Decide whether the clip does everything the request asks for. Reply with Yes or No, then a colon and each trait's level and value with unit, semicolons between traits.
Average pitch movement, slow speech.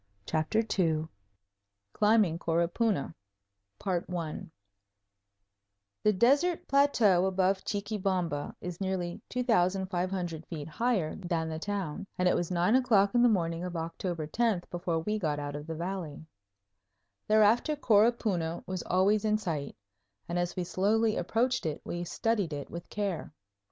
Yes: average, 4.5 semitones; slow, 130 wpm